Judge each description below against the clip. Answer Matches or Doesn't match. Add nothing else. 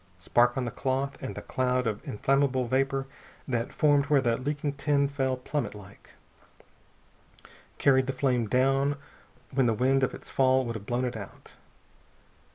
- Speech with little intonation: Matches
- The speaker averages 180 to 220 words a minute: Doesn't match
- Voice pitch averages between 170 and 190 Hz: Doesn't match